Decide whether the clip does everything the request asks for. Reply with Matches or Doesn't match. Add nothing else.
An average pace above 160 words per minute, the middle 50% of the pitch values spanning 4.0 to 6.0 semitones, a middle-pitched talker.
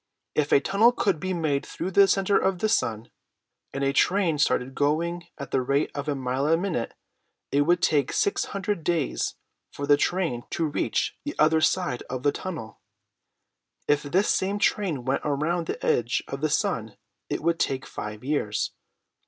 Matches